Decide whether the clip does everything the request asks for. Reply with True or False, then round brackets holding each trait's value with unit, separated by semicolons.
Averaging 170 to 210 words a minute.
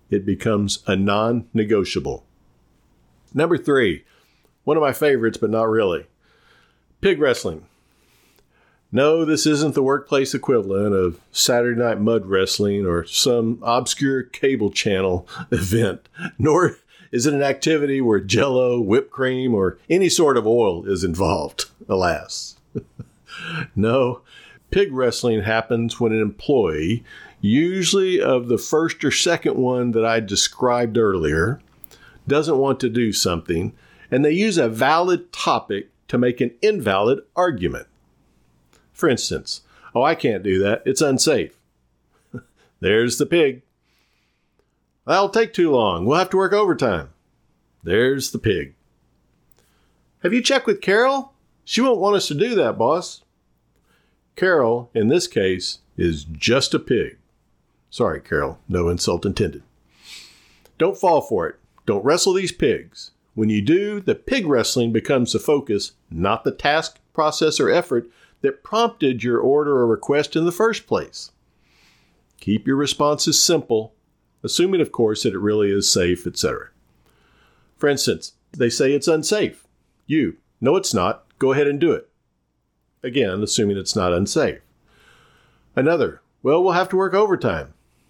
False (140 wpm)